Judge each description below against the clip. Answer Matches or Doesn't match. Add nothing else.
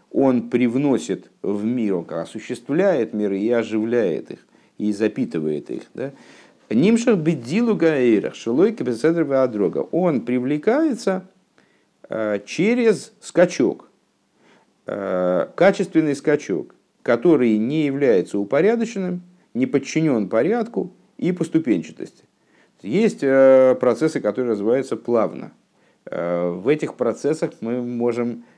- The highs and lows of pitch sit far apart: Matches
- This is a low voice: Matches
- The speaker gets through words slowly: Matches